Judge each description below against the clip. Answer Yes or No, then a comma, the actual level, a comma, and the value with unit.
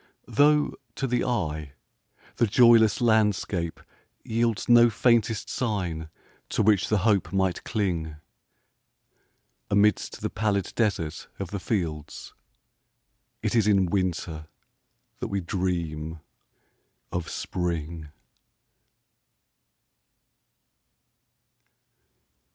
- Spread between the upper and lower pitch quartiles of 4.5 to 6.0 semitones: Yes, average, 4.9 semitones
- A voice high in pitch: No, low, 100 Hz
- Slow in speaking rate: Yes, slow, 80 wpm